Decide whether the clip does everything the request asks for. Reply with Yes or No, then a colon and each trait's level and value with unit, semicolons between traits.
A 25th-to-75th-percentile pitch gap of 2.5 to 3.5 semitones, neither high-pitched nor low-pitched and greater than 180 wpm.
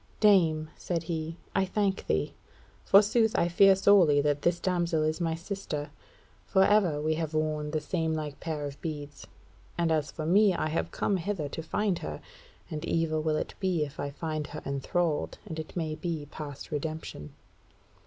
No: average, 2.8 semitones; medium, 160 Hz; average, 175 wpm